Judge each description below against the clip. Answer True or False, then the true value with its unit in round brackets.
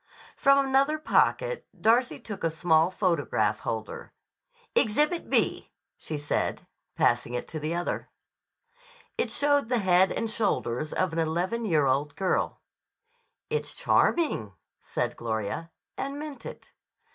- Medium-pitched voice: True (180 Hz)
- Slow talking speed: True (130 wpm)